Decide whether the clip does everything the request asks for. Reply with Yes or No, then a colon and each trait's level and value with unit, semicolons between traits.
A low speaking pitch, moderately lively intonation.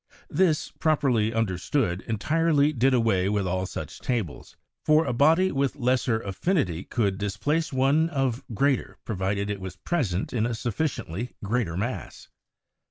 No: low, 120 Hz; wide, 6.4 semitones